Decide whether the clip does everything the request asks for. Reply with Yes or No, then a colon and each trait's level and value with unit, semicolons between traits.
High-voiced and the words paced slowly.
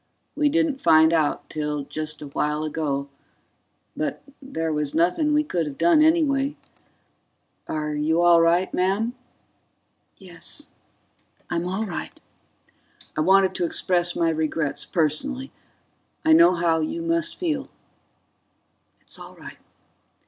No: medium, 175 Hz; slow, 125 wpm